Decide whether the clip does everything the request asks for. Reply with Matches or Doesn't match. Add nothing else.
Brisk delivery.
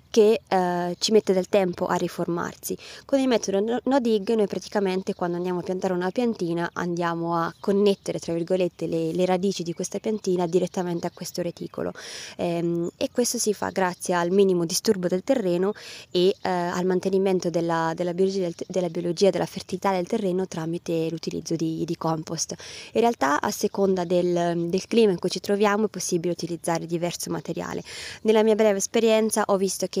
Matches